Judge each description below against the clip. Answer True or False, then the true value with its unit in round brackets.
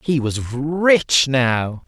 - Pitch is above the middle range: False (140 Hz)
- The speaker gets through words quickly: False (130 wpm)